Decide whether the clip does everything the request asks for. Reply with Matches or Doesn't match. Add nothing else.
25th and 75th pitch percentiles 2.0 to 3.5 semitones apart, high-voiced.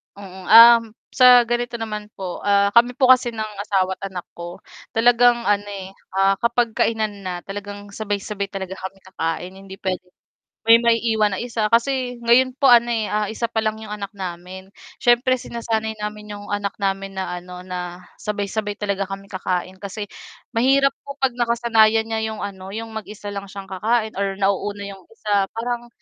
Matches